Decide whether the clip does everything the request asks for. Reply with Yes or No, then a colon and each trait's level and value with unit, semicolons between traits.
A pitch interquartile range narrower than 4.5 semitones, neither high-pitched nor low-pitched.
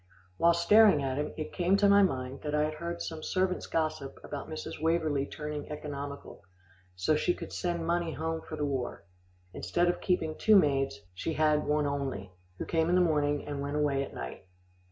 Yes: average, 3.2 semitones; medium, 150 Hz